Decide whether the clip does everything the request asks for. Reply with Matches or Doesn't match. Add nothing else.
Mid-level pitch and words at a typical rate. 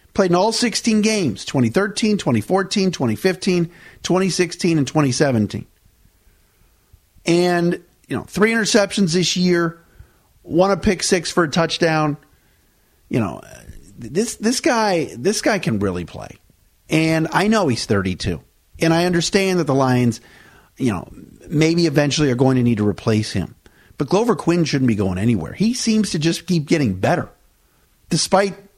Matches